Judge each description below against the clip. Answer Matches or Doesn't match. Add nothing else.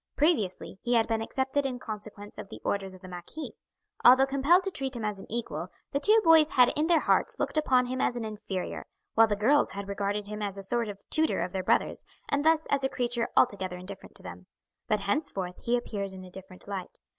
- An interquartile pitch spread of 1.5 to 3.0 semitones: Doesn't match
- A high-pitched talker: Matches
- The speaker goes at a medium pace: Doesn't match